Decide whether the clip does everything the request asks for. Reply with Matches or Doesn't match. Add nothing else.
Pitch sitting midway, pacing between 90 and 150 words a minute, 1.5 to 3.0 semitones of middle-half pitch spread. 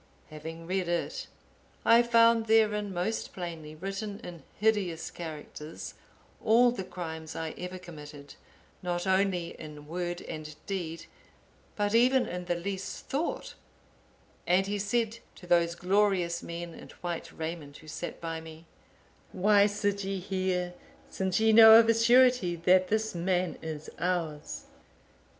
Doesn't match